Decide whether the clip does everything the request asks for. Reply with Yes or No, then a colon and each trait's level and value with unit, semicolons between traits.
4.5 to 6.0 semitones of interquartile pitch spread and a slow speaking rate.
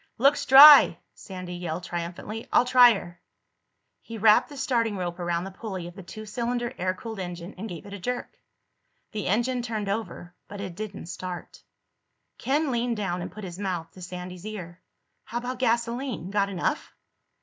No: average, 4.8 semitones; average, 175 wpm